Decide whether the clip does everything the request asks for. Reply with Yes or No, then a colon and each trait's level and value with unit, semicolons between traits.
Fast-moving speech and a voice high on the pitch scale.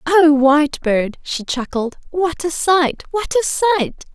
No: average, 145 wpm; very high, 310 Hz